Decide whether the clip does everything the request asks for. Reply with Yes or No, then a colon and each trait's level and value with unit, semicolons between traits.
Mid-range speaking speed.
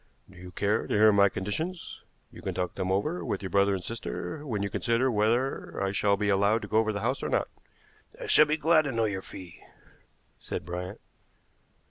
No: fast, 210 wpm